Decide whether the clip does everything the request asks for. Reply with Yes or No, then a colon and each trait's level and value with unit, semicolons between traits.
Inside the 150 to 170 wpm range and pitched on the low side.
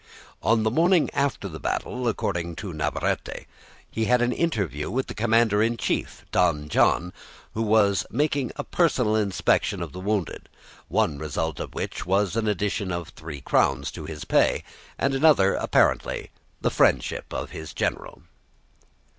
Yes: average, 155 wpm; low, 105 Hz